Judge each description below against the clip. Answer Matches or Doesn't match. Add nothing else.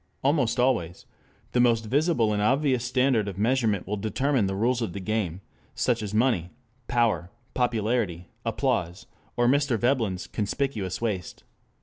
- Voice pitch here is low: Matches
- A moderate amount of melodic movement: Matches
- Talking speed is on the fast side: Doesn't match